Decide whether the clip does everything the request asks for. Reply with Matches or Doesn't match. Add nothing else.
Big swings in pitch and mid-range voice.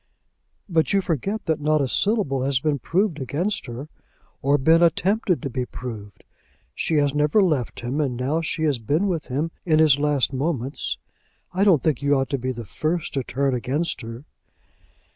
Doesn't match